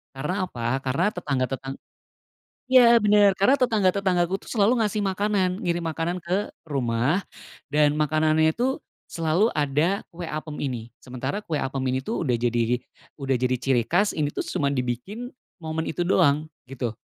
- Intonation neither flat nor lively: No, wide, 6.6 semitones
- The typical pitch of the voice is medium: Yes, medium, 160 Hz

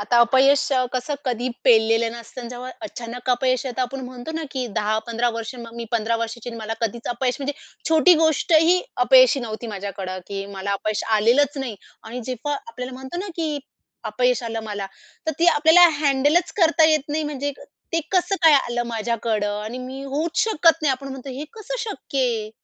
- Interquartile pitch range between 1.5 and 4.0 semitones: No, average, 4.4 semitones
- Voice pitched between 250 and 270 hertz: Yes, very high, 255 Hz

